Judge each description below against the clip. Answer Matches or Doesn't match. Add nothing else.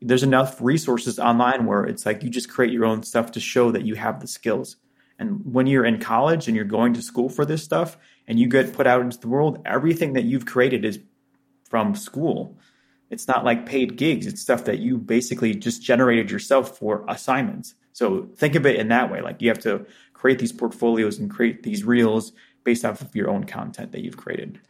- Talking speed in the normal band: Doesn't match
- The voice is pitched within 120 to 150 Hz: Matches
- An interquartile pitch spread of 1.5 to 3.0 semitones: Matches